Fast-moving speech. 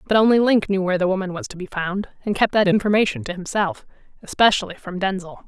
Yes: fast, 210 wpm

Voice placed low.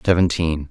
Yes: very low, 80 Hz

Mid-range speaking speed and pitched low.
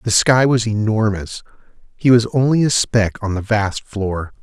Yes: average, 175 wpm; low, 110 Hz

